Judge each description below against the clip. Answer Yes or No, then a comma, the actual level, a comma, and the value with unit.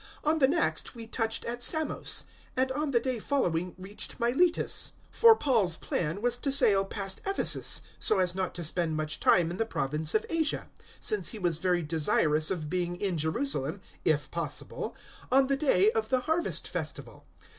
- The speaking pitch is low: No, high, 215 Hz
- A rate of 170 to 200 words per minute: Yes, average, 180 wpm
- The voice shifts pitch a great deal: Yes, wide, 7.7 semitones